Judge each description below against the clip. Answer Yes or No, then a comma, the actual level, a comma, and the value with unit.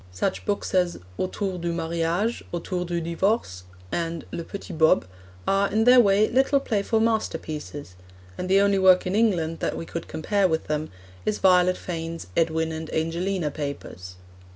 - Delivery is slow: No, average, 160 wpm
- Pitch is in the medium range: Yes, medium, 175 Hz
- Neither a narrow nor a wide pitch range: Yes, average, 3.5 semitones